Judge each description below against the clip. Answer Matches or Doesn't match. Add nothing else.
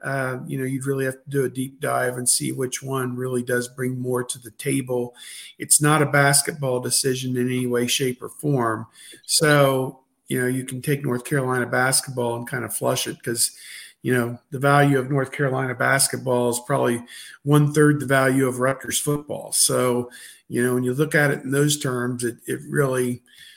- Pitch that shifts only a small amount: Matches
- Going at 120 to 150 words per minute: Doesn't match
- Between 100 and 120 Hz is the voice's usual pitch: Doesn't match